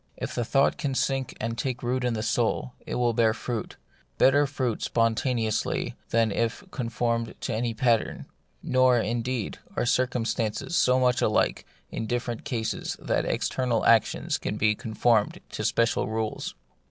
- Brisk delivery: No, average, 155 wpm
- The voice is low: Yes, low, 120 Hz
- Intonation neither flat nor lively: No, narrow, 2.1 semitones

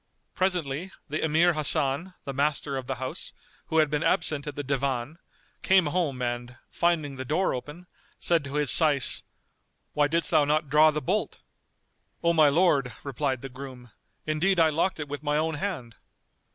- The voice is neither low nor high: Yes, medium, 150 Hz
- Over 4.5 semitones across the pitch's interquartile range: No, average, 3.1 semitones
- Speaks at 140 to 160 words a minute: No, average, 180 wpm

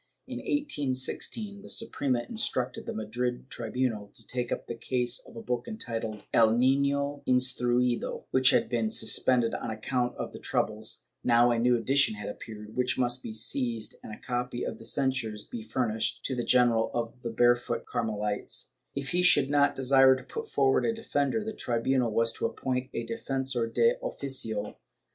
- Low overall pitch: Yes, low, 125 Hz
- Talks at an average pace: Yes, average, 175 wpm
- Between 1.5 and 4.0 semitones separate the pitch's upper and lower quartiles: Yes, narrow, 2.6 semitones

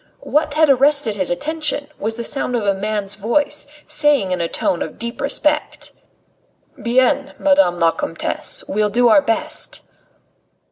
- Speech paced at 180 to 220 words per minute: No, average, 150 wpm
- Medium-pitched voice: No, high, 245 Hz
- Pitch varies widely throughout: Yes, wide, 6.1 semitones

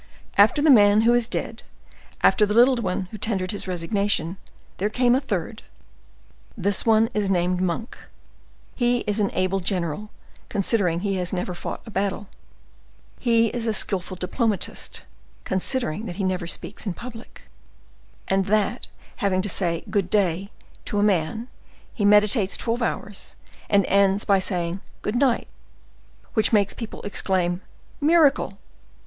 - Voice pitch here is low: No, high, 205 Hz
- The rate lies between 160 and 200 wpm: No, average, 150 wpm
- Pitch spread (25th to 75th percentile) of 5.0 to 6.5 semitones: No, average, 3.3 semitones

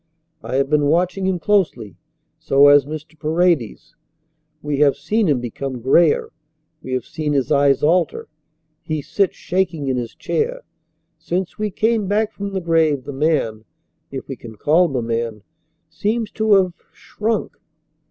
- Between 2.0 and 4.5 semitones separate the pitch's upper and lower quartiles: No, wide, 5.6 semitones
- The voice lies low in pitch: No, medium, 155 Hz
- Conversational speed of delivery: Yes, average, 160 wpm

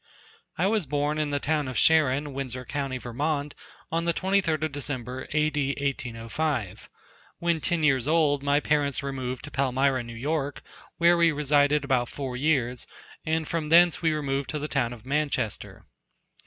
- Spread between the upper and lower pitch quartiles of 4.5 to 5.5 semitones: No, average, 2.9 semitones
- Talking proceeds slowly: No, average, 165 wpm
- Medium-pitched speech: Yes, medium, 145 Hz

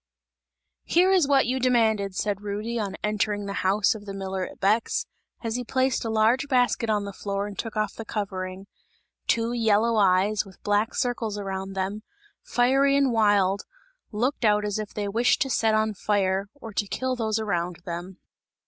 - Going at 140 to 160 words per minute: No, average, 185 wpm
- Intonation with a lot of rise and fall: No, average, 2.8 semitones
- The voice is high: Yes, high, 210 Hz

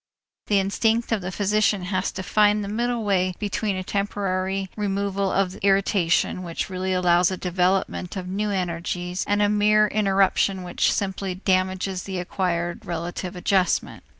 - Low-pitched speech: No, high, 190 Hz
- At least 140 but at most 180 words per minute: Yes, average, 150 wpm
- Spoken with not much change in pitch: Yes, narrow, 1.9 semitones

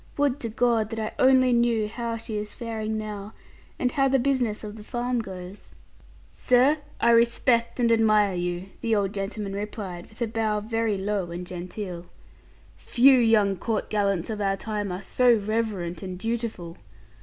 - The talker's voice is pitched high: Yes, high, 215 Hz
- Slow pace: No, average, 170 wpm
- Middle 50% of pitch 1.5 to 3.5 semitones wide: Yes, average, 2.9 semitones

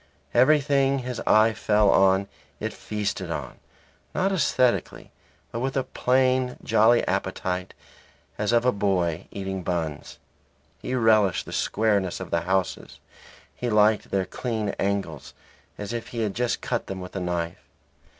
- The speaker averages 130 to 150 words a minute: Yes, average, 145 wpm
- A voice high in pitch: No, low, 105 Hz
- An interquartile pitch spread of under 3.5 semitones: No, average, 4.5 semitones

